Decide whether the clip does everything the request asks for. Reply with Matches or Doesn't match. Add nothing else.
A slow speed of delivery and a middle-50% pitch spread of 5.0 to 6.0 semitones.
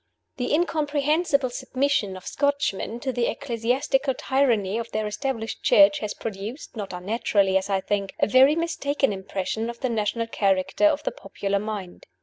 Doesn't match